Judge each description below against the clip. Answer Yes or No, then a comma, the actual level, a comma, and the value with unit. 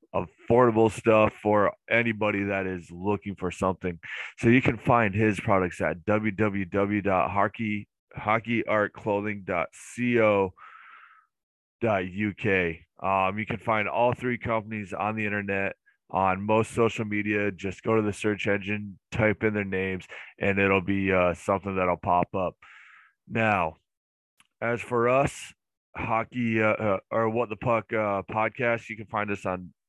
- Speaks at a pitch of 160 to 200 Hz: No, low, 105 Hz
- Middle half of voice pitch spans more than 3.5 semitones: No, narrow, 2.6 semitones